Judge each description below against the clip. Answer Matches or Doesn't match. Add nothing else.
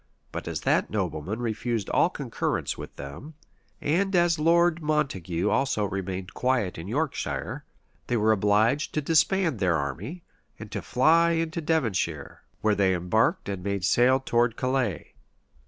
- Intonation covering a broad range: Matches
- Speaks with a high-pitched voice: Doesn't match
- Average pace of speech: Matches